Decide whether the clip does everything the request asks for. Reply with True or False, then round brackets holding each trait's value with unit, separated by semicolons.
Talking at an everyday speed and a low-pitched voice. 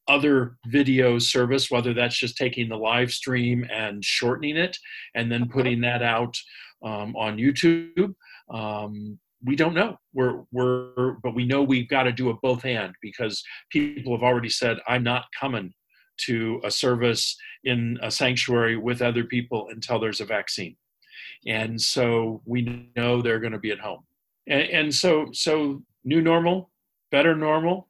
True (165 wpm; 125 Hz)